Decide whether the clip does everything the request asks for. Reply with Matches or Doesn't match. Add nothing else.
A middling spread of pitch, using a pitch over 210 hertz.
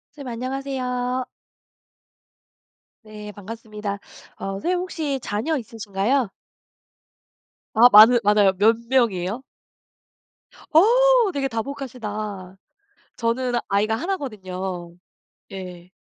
Matches